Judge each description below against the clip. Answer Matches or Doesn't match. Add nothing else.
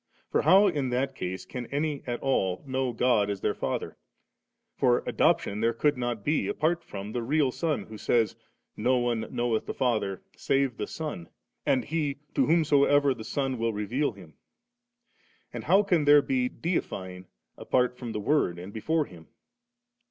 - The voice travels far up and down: Doesn't match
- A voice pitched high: Doesn't match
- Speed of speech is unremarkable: Matches